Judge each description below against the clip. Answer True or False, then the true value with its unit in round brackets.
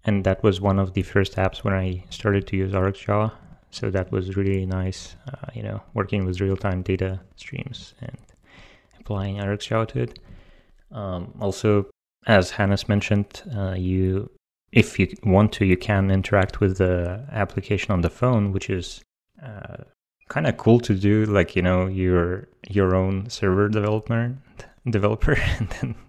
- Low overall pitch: True (100 Hz)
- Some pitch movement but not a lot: False (2.1 semitones)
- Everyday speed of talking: True (165 wpm)